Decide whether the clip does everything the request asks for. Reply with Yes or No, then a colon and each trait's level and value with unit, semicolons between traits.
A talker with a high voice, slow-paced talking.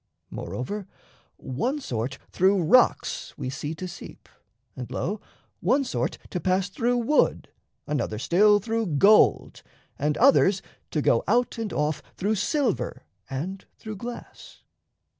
Yes: high, 195 Hz; slow, 130 wpm